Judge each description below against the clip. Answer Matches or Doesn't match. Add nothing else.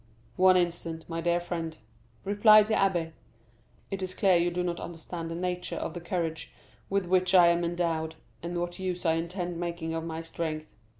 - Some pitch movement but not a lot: Doesn't match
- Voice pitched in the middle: Matches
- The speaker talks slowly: Doesn't match